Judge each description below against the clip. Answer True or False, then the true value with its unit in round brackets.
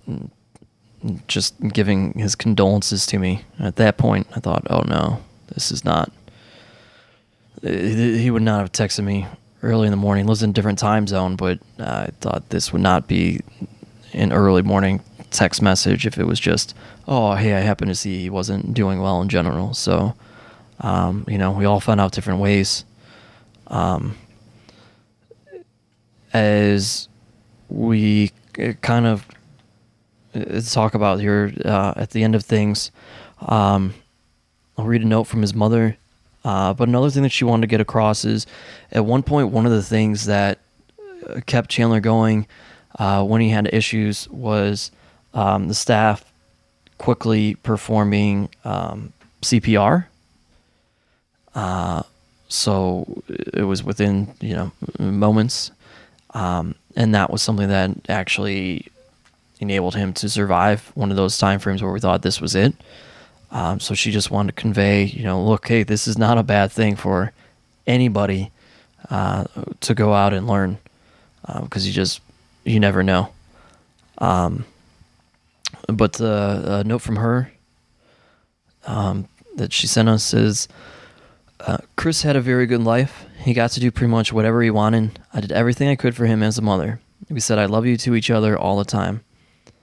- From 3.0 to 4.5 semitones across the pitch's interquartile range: False (2.4 semitones)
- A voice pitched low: True (105 Hz)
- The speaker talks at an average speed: True (160 wpm)